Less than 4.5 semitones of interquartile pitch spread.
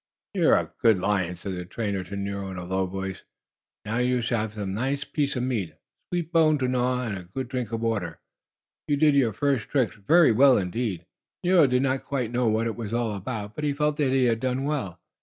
No: average, 5.1 semitones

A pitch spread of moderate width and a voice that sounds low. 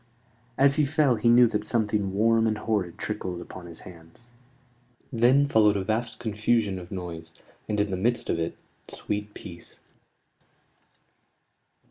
Yes: average, 4.1 semitones; low, 105 Hz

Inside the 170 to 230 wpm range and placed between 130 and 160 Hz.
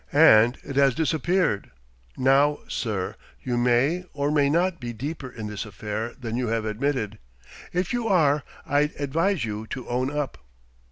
No: average, 160 wpm; low, 135 Hz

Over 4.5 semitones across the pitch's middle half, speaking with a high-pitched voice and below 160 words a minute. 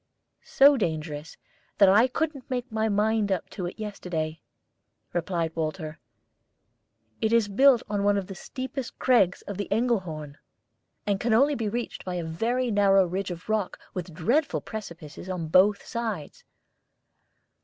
Yes: average, 4.9 semitones; high, 200 Hz; average, 150 wpm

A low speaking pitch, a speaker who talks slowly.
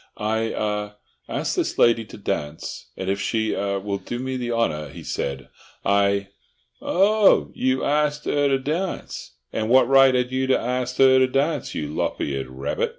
No: low, 115 Hz; average, 160 wpm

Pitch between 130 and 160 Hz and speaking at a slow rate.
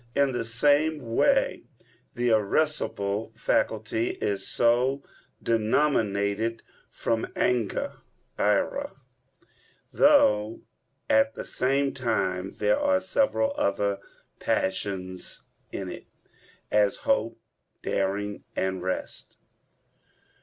No: low, 110 Hz; slow, 90 wpm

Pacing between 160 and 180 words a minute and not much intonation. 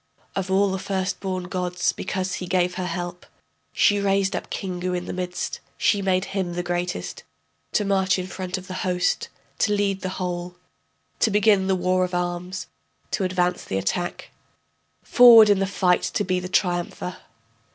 Yes: average, 175 wpm; narrow, 1.4 semitones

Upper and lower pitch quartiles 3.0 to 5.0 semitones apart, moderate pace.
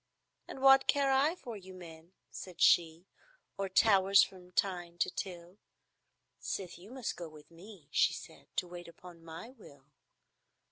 Yes: average, 3.6 semitones; average, 155 wpm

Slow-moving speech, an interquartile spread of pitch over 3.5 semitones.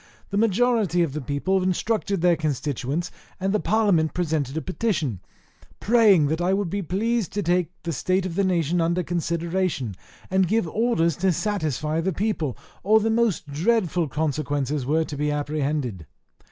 No: average, 165 wpm; average, 4.7 semitones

